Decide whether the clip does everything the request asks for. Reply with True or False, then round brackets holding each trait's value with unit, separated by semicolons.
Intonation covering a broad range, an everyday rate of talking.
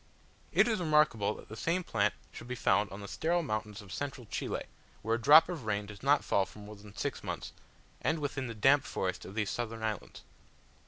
False (5.8 semitones; 215 wpm)